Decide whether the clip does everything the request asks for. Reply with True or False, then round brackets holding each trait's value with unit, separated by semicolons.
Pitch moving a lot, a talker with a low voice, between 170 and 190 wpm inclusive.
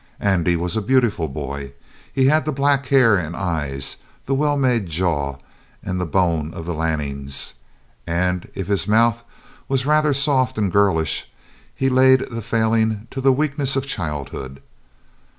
False (8.2 semitones; 100 Hz; 155 wpm)